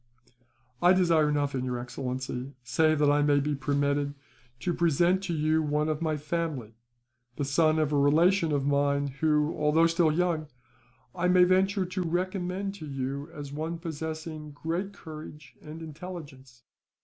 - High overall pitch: No, medium, 155 Hz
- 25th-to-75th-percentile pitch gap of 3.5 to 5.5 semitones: No, average, 2.9 semitones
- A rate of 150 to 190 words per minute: Yes, average, 155 wpm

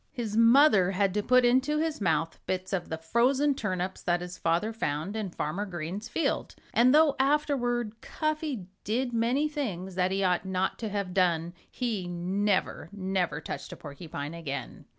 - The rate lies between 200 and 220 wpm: No, average, 170 wpm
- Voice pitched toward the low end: No, high, 200 Hz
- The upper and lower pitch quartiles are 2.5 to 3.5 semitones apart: No, wide, 5.5 semitones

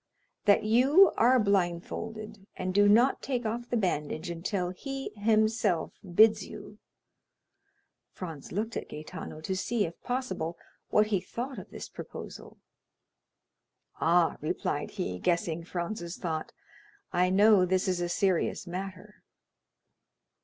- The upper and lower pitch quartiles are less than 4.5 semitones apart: Yes, average, 4.1 semitones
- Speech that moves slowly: Yes, slow, 125 wpm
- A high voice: Yes, high, 195 Hz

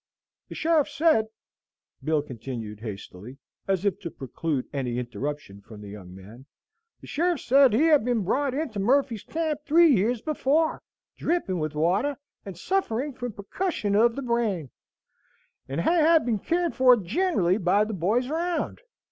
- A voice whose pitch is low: No, high, 220 Hz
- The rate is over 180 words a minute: No, average, 155 wpm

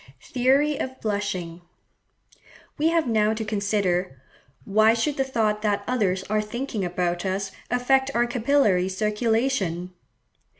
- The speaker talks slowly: Yes, slow, 120 wpm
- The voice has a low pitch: No, high, 215 Hz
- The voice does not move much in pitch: No, average, 4.6 semitones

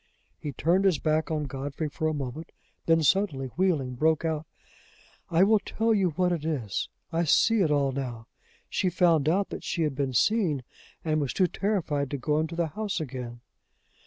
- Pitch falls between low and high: Yes, medium, 155 Hz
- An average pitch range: Yes, average, 4.2 semitones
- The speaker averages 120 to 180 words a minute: No, average, 190 wpm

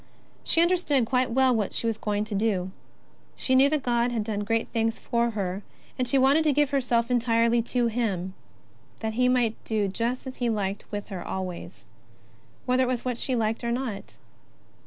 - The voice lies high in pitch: Yes, high, 235 Hz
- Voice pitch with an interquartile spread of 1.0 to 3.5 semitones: Yes, average, 2.9 semitones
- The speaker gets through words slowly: No, average, 195 wpm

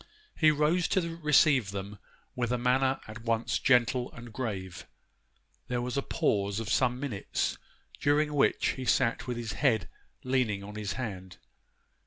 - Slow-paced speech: No, average, 155 wpm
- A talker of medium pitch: No, low, 120 Hz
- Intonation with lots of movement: No, average, 4.2 semitones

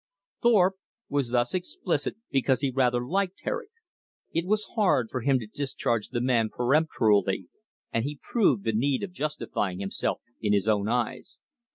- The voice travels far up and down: Yes, wide, 6.6 semitones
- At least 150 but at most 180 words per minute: Yes, average, 160 wpm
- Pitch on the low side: Yes, low, 130 Hz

